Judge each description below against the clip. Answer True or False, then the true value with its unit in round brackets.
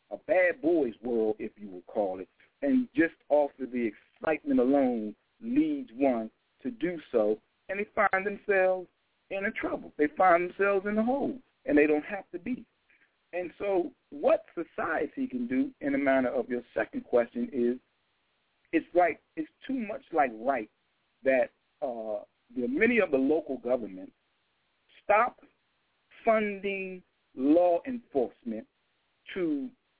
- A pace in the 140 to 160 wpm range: True (150 wpm)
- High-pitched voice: True (200 Hz)